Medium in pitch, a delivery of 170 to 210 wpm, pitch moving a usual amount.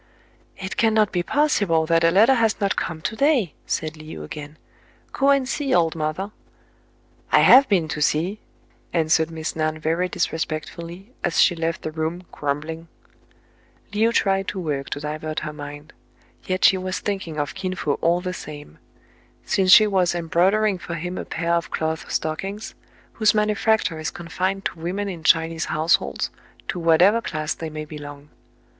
Yes: medium, 170 Hz; average, 175 wpm; average, 3.8 semitones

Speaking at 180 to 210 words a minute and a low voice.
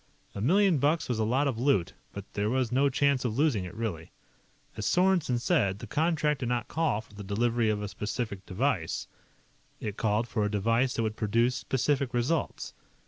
Yes: average, 195 wpm; low, 120 Hz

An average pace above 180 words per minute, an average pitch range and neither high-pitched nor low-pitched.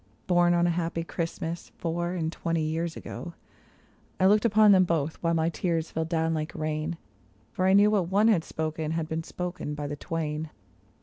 No: average, 190 wpm; narrow, 1.9 semitones; medium, 165 Hz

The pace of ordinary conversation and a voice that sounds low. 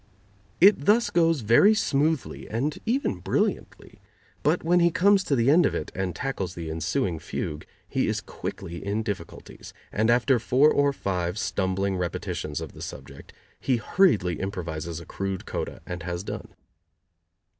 Yes: average, 155 wpm; low, 105 Hz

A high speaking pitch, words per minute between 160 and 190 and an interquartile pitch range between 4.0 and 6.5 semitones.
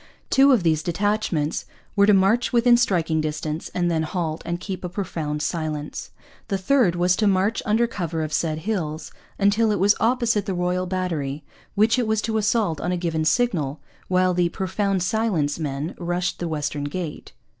No: medium, 180 Hz; average, 180 wpm; average, 4.7 semitones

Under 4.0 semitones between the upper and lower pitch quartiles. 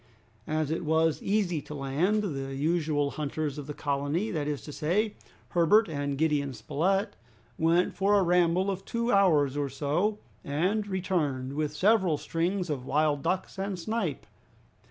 No: average, 4.7 semitones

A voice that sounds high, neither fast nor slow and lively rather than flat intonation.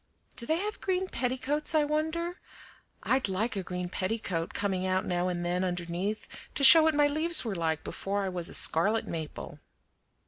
Yes: high, 205 Hz; average, 180 wpm; wide, 8.8 semitones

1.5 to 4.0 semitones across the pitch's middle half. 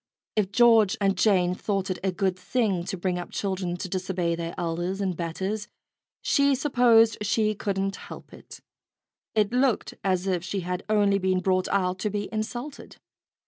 Yes: average, 2.8 semitones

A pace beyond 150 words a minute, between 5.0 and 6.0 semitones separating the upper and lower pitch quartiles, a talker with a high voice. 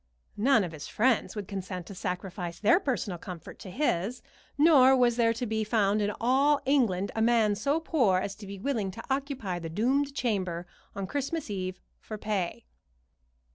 Yes: average, 175 wpm; wide, 5.6 semitones; high, 215 Hz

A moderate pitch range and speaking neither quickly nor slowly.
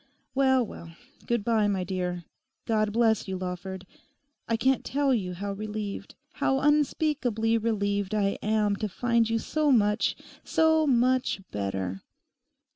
No: average, 4.1 semitones; slow, 130 wpm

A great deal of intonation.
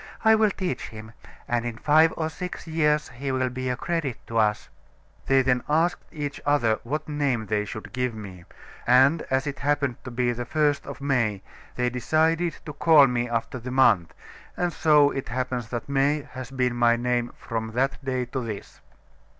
No: average, 3.6 semitones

